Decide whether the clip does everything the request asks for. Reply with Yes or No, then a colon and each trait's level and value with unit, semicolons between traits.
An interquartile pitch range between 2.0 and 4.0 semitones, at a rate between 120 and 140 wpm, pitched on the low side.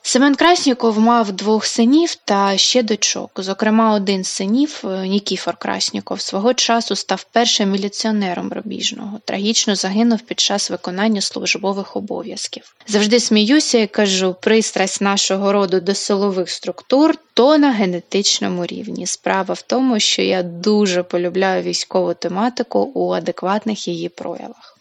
No: average, 3.4 semitones; average, 130 wpm; high, 205 Hz